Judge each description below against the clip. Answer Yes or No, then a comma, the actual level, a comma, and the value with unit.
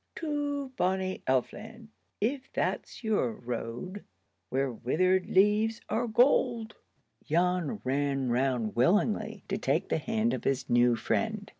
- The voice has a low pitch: No, high, 190 Hz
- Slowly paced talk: Yes, slow, 130 wpm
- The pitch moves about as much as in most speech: No, wide, 8.8 semitones